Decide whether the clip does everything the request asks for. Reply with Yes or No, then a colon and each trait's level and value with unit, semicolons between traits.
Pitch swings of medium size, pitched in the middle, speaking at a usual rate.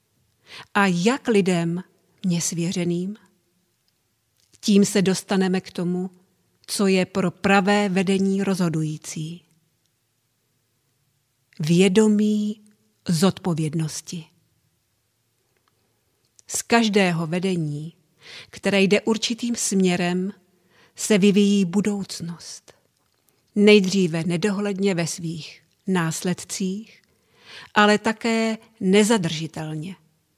No: average, 4.1 semitones; medium, 180 Hz; slow, 70 wpm